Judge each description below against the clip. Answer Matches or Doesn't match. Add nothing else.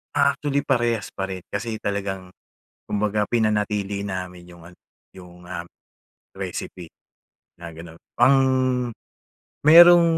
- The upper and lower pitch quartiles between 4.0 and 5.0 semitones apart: Matches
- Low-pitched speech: Matches